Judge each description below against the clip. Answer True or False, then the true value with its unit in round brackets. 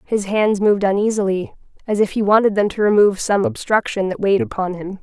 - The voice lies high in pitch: True (205 Hz)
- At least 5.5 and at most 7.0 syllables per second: True (6.1 syllables/s)